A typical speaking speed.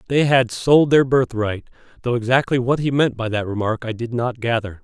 No: fast, 210 wpm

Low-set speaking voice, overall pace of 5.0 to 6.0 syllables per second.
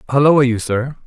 Yes: low, 130 Hz; 5.5 syllables/s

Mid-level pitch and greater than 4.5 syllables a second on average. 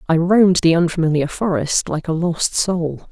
Yes: medium, 170 Hz; 4.8 syllables/s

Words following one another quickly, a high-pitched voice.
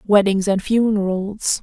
No: slow, 110 wpm; high, 200 Hz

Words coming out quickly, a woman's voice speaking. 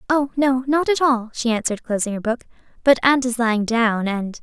Yes: fast, 215 wpm; female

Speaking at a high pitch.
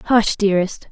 Yes: high, 205 Hz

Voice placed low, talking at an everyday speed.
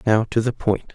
No: low, 110 Hz; fast, 255 wpm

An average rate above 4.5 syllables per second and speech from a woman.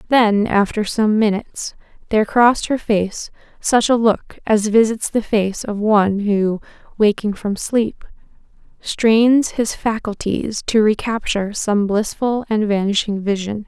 No: 4.1 syllables/s; female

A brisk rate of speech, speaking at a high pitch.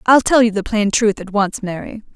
Yes: fast, 250 wpm; high, 210 Hz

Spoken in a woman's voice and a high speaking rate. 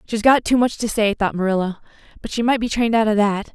Yes: female; fast, 270 wpm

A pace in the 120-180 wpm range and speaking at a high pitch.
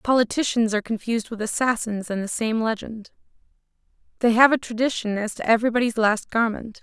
Yes: average, 160 wpm; high, 225 Hz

